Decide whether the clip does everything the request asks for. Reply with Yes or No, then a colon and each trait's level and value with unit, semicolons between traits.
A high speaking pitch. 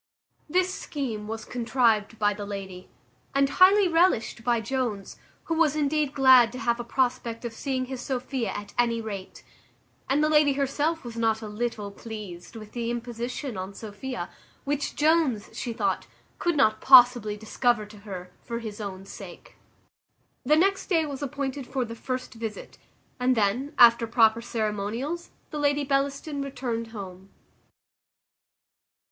Yes: high, 240 Hz